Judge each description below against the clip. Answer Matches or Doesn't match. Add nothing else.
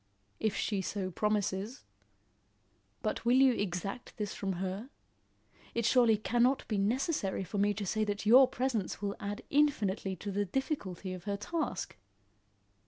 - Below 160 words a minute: Matches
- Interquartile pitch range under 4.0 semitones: Matches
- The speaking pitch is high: Matches